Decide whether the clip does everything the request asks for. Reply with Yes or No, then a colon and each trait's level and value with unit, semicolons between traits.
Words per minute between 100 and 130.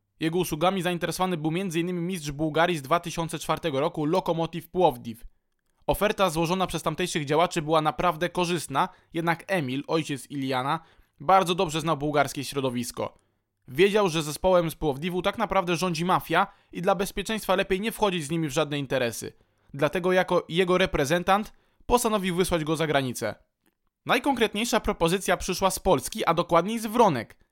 No: average, 145 wpm